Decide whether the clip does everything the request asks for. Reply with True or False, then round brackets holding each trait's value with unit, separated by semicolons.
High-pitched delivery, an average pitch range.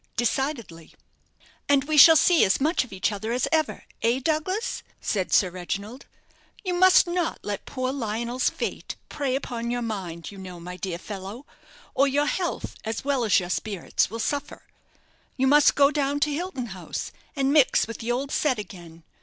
False (250 Hz; 6.2 semitones)